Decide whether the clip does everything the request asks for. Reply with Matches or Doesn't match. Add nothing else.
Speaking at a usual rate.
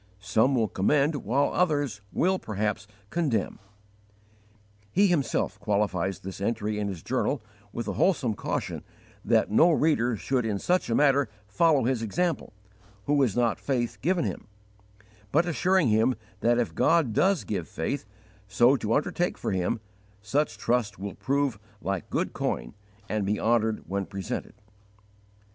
Matches